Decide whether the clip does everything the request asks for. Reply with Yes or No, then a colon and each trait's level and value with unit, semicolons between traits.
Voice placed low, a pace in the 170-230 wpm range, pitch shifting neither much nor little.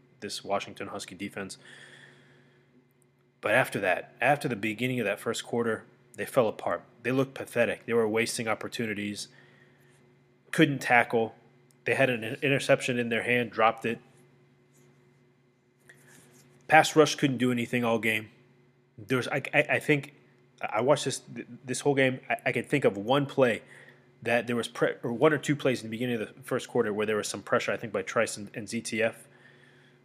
No: low, 125 Hz; average, 175 wpm; narrow, 1.6 semitones